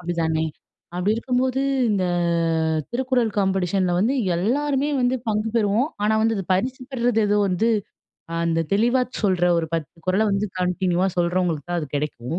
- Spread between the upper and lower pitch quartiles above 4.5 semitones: Yes, average, 5.3 semitones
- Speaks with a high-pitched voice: Yes, high, 195 Hz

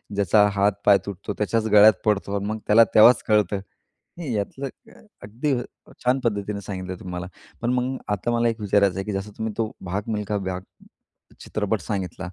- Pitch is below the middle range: Yes, low, 105 Hz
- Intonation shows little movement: Yes, narrow, 2.1 semitones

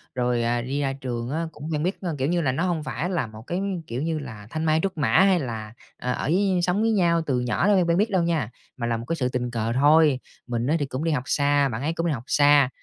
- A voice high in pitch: No, medium, 145 Hz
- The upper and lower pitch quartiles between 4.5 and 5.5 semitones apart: Yes, average, 5.2 semitones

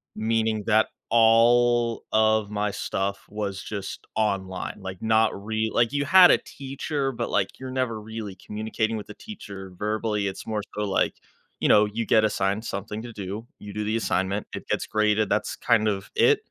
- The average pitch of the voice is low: Yes, low, 110 Hz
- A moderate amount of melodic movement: No, narrow, 1.8 semitones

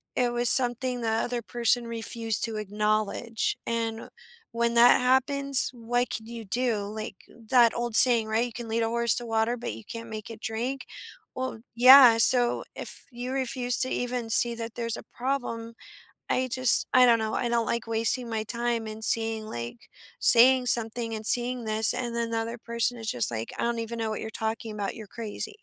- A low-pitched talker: No, high, 230 Hz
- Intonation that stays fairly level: Yes, narrow, 1.6 semitones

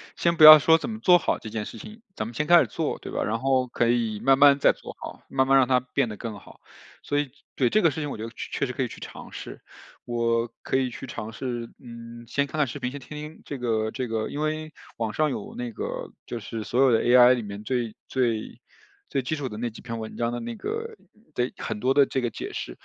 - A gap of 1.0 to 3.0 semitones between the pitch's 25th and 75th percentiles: No, average, 3.7 semitones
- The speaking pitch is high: No, low, 125 Hz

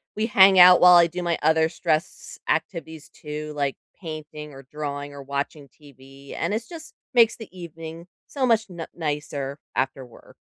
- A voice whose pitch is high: No, medium, 160 Hz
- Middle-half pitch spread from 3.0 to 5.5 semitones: Yes, average, 3.9 semitones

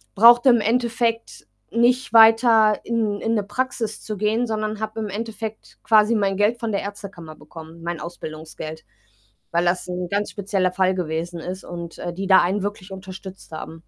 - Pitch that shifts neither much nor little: Yes, average, 3.8 semitones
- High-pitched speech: Yes, high, 205 Hz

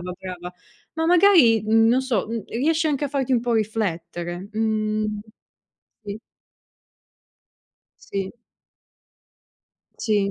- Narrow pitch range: No, average, 4.6 semitones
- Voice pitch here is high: Yes, high, 220 Hz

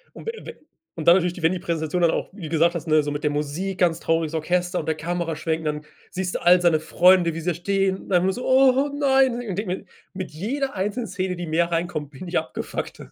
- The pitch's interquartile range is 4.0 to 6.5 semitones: No, average, 2.9 semitones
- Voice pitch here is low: No, medium, 175 Hz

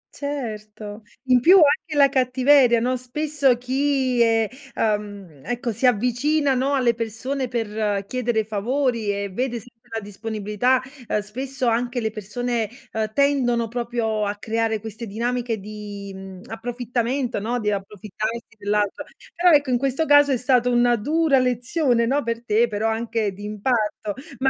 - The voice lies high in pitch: Yes, high, 235 Hz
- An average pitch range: Yes, average, 3.2 semitones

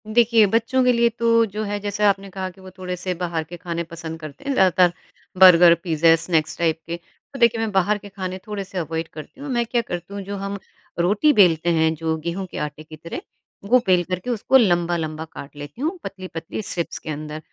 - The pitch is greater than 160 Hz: Yes, medium, 185 Hz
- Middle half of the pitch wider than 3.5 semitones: Yes, average, 4.1 semitones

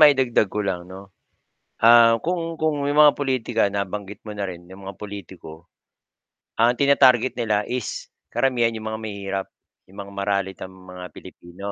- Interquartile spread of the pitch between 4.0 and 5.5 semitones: Yes, average, 4.4 semitones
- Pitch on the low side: Yes, low, 105 Hz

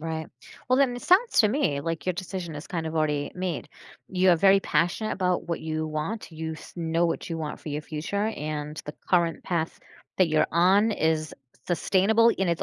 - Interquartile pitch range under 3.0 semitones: No, average, 3.5 semitones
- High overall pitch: No, medium, 170 Hz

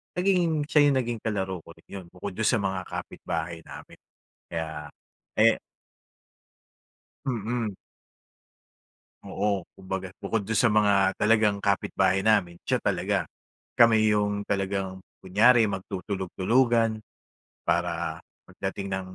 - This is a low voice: Yes, low, 100 Hz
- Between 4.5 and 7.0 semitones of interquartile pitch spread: No, average, 3.0 semitones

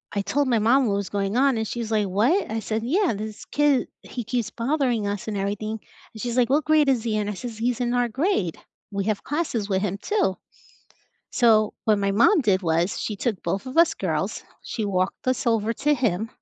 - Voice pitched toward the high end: Yes, high, 225 Hz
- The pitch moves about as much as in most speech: Yes, average, 4.0 semitones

